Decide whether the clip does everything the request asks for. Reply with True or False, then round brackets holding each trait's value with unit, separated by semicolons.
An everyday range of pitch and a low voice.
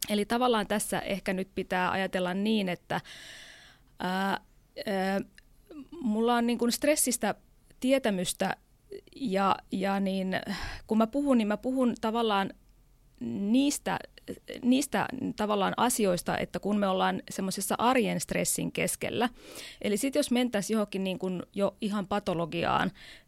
False (4.0 semitones; 210 Hz)